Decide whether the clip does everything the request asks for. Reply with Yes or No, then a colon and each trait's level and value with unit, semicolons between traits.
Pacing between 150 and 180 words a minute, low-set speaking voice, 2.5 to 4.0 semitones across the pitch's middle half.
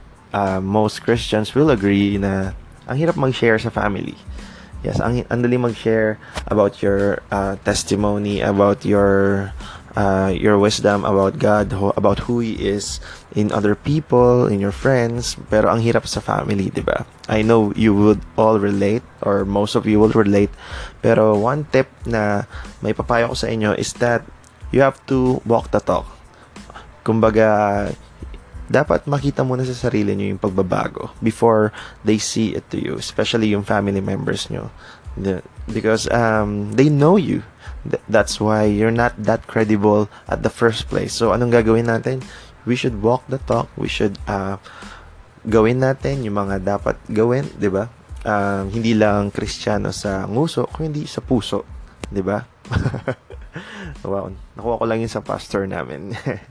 Yes: fast, 155 wpm; low, 110 Hz; average, 2.8 semitones